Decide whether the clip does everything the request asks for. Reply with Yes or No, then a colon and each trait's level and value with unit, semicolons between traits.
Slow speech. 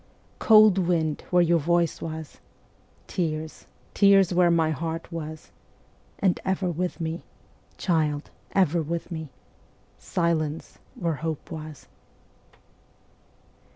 Yes: slow, 105 wpm